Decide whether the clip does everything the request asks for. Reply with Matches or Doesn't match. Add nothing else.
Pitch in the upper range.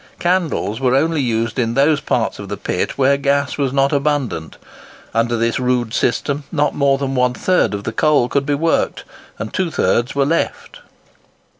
Doesn't match